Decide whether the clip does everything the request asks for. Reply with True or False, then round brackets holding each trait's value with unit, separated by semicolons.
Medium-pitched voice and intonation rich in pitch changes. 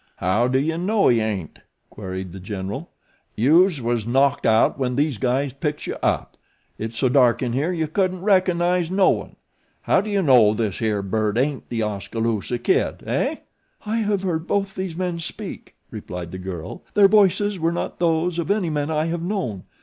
True (145 Hz; 8.1 semitones)